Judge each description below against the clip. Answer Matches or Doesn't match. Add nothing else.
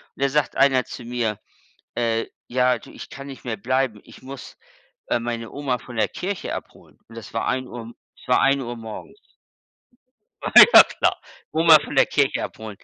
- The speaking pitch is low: Matches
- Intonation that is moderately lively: Matches